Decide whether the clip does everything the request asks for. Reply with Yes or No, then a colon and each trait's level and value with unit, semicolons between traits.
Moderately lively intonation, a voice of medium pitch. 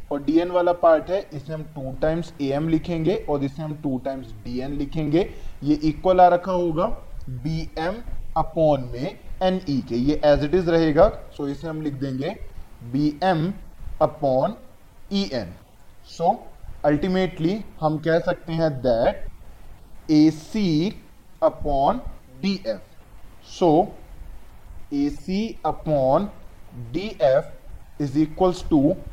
Yes: average, 3.5 semitones; medium, 155 Hz